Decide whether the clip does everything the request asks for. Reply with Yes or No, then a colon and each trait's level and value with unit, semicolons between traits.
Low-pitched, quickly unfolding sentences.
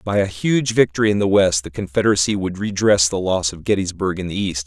Yes: very low, 95 Hz; fast, 230 wpm